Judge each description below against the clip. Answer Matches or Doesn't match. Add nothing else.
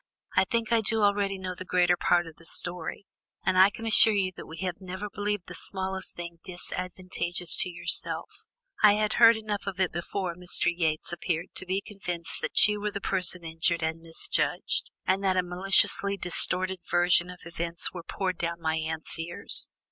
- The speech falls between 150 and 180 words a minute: Doesn't match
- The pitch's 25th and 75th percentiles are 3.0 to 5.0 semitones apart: Doesn't match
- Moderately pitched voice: Matches